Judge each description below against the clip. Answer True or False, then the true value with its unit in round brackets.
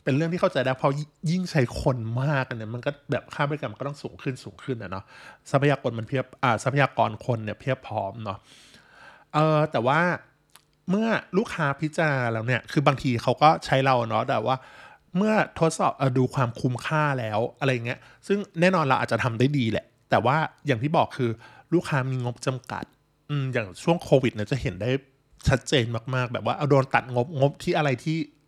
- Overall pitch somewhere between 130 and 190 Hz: True (135 Hz)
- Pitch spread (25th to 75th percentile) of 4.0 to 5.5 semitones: False (3.5 semitones)